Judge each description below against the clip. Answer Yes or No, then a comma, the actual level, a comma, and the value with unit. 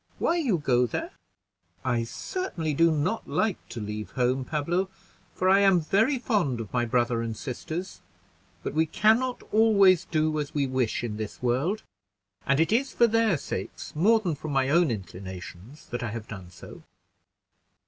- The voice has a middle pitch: Yes, medium, 150 Hz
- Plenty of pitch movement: Yes, wide, 8.4 semitones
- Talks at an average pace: Yes, average, 175 wpm